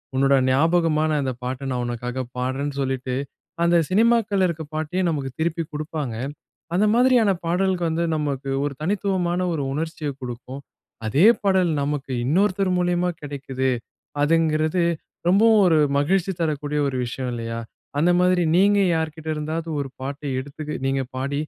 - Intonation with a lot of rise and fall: No, average, 4.6 semitones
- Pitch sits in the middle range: Yes, medium, 155 Hz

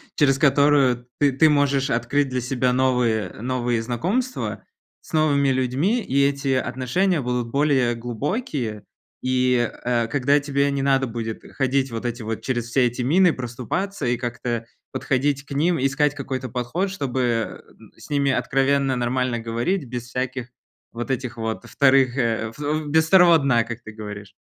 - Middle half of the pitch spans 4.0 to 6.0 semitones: No, average, 2.8 semitones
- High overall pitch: No, low, 130 Hz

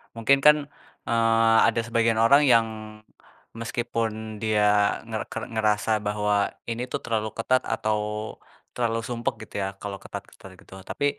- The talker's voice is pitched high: No, low, 115 Hz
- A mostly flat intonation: Yes, narrow, 1.5 semitones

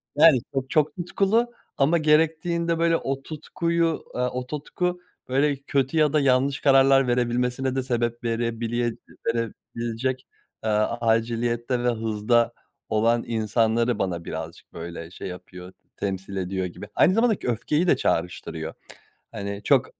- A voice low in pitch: Yes, low, 125 Hz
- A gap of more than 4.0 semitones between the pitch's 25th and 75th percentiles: Yes, average, 4.8 semitones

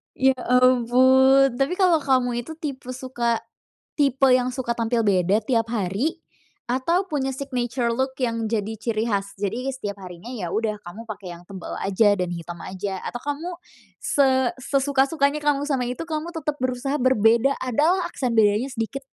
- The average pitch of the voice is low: No, very high, 250 Hz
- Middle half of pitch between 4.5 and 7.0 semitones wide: No, average, 3.6 semitones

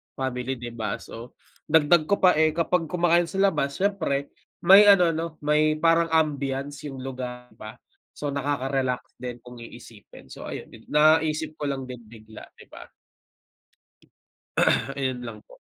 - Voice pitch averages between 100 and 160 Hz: Yes, medium, 140 Hz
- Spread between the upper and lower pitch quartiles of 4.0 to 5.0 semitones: Yes, average, 4.5 semitones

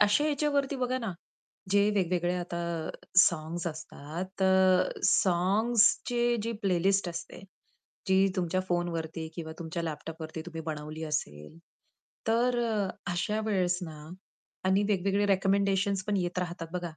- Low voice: No, medium, 185 Hz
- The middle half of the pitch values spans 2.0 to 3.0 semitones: No, average, 3.4 semitones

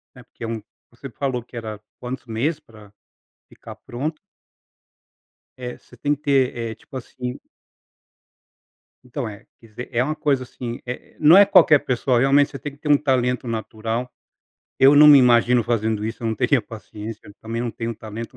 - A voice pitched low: Yes, low, 125 Hz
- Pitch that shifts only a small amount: No, average, 3.2 semitones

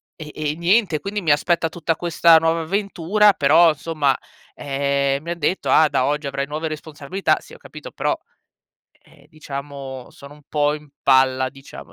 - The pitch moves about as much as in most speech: Yes, average, 3.0 semitones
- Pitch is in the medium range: Yes, medium, 150 Hz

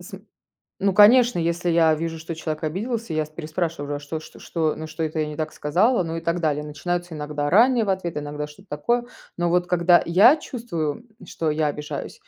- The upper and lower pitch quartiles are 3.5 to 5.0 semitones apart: No, average, 3.1 semitones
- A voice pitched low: No, medium, 165 Hz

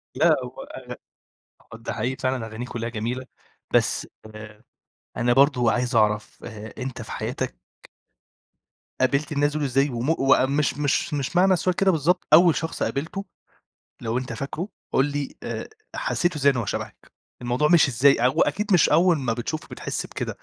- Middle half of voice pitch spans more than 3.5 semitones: Yes, average, 4.6 semitones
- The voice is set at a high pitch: No, low, 135 Hz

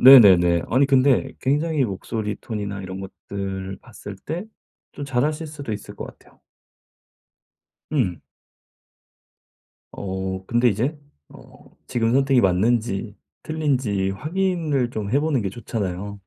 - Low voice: Yes, low, 115 Hz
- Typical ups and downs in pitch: No, wide, 6.1 semitones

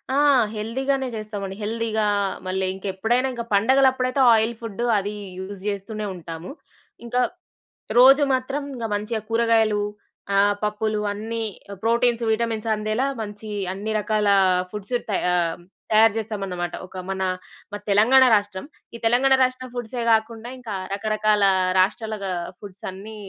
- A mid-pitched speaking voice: No, high, 215 Hz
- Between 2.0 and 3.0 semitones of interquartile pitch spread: Yes, narrow, 2.5 semitones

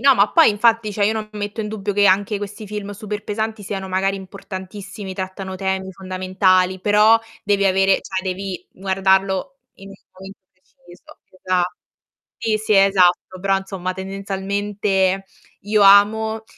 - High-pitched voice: Yes, high, 195 Hz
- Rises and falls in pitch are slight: Yes, narrow, 1.6 semitones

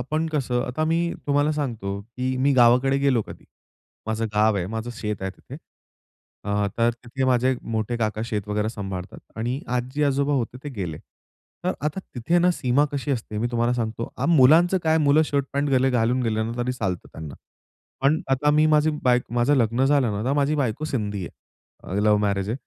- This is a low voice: Yes, low, 125 Hz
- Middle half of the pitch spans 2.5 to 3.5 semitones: No, average, 4.4 semitones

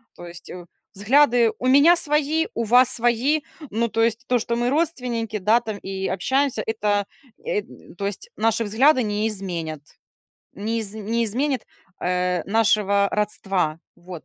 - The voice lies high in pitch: Yes, high, 225 Hz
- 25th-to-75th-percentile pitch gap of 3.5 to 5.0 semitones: Yes, average, 3.9 semitones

